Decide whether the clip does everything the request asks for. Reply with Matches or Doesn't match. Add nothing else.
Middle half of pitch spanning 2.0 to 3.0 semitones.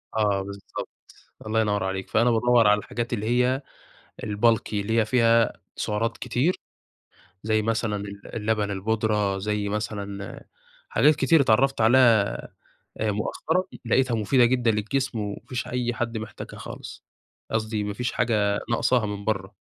Matches